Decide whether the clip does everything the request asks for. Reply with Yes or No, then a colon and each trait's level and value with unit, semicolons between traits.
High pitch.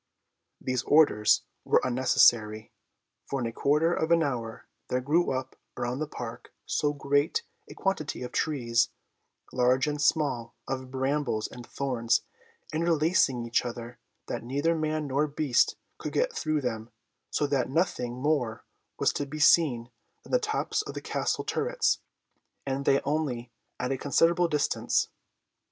No: medium, 140 Hz